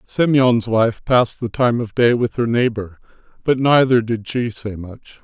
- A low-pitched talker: Yes, low, 115 Hz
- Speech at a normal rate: Yes, average, 185 wpm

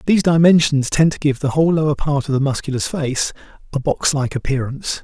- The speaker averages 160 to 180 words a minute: No, fast, 205 wpm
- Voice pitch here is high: No, medium, 145 Hz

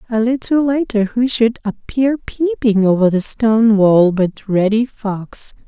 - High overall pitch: Yes, high, 225 Hz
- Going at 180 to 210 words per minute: No, average, 150 wpm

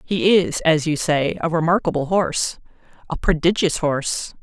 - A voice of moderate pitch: Yes, medium, 165 Hz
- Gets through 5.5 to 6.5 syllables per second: No, 4.9 syllables/s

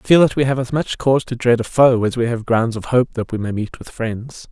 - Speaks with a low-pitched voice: Yes, low, 120 Hz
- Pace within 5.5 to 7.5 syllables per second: Yes, 5.7 syllables/s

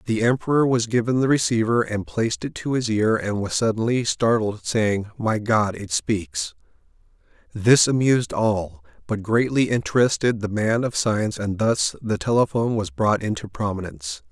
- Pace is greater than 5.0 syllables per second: No, 4.9 syllables/s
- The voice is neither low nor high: No, low, 115 Hz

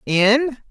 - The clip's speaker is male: No, female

